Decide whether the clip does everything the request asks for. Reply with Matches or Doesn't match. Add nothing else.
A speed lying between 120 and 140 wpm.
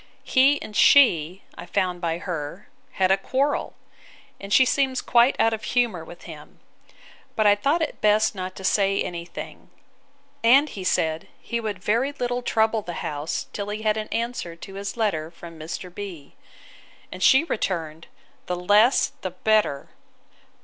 Doesn't match